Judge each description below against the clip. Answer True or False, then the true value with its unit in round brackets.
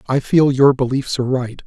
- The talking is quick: True (215 wpm)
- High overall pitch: False (130 Hz)